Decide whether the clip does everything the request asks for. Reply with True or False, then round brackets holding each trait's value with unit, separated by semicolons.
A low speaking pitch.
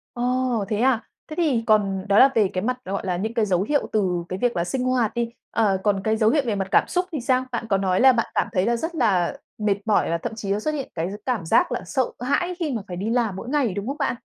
False (225 Hz)